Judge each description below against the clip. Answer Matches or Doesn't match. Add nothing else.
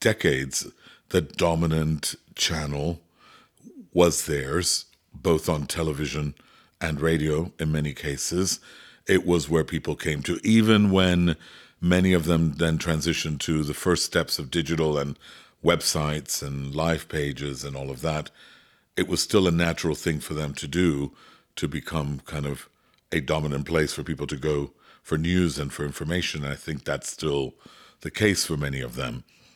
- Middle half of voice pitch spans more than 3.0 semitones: Doesn't match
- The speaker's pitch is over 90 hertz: Doesn't match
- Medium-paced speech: Matches